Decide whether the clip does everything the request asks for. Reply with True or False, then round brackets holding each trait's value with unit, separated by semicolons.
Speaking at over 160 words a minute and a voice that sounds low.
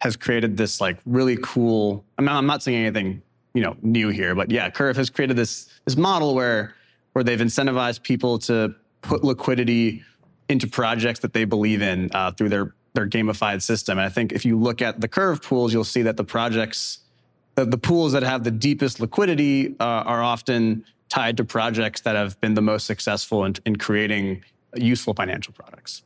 True (195 wpm; 115 Hz)